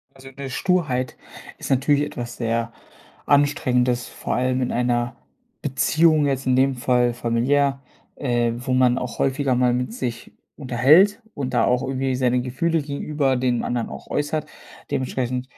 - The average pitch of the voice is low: Yes, low, 130 Hz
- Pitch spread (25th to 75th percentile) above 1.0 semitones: Yes, narrow, 2.4 semitones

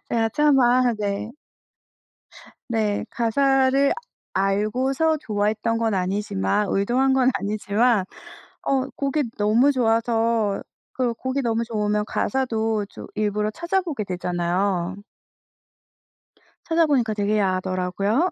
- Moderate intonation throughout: Yes, average, 4.2 semitones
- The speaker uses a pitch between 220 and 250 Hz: Yes, high, 225 Hz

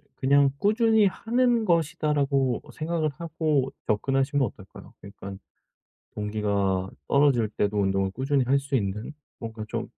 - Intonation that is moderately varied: No, wide, 6.7 semitones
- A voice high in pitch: No, low, 135 Hz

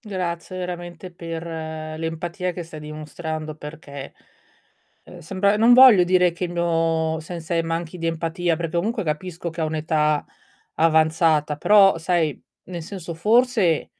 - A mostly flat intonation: Yes, narrow, 2.2 semitones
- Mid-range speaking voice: Yes, medium, 165 Hz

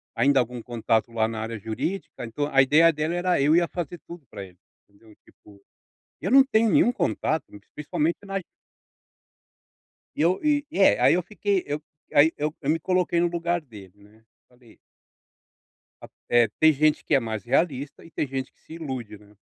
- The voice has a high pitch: No, medium, 150 Hz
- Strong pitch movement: Yes, wide, 6.6 semitones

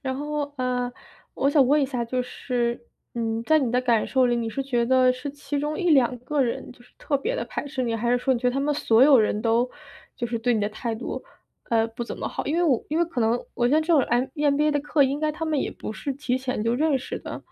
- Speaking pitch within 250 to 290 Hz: Yes, very high, 255 Hz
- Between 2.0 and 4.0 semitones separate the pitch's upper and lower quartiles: Yes, average, 3.4 semitones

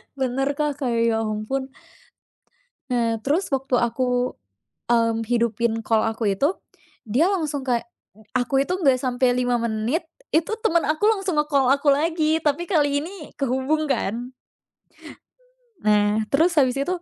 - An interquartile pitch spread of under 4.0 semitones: No, average, 4.3 semitones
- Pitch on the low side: No, very high, 265 Hz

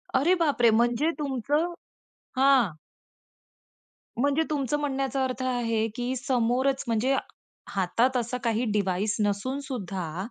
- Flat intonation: No, average, 3.4 semitones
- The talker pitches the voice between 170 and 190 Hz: No, very high, 250 Hz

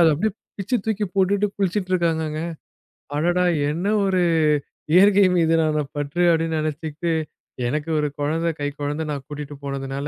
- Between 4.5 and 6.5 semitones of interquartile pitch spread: No, average, 3.7 semitones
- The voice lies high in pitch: No, medium, 160 Hz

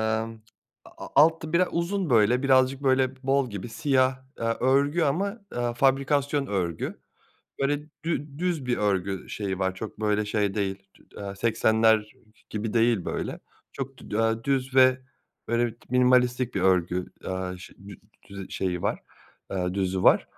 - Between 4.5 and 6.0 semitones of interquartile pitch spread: Yes, average, 5.2 semitones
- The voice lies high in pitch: No, low, 120 Hz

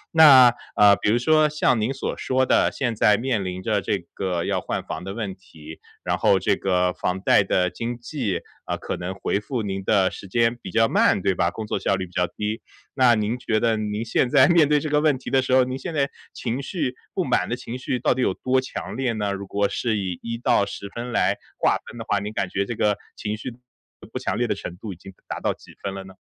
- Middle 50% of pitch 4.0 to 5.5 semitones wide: Yes, average, 4.5 semitones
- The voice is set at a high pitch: No, low, 110 Hz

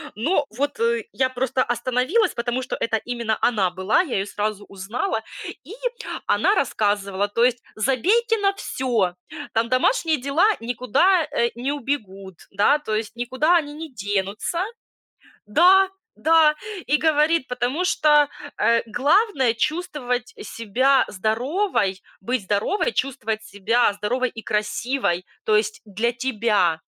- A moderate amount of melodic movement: No, wide, 5.7 semitones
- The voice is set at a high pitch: Yes, high, 245 Hz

